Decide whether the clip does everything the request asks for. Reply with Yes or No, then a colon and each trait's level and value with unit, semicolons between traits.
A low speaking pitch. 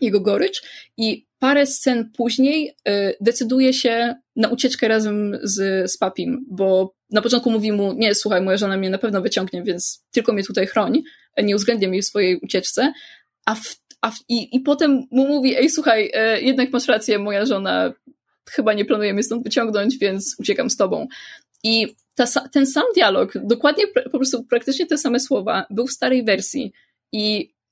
No: high, 235 Hz